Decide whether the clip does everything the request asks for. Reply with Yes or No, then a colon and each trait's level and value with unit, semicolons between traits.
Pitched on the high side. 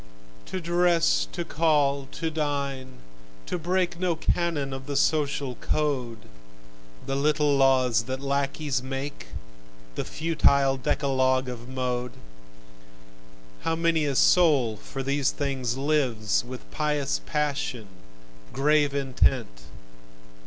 No: medium, 140 Hz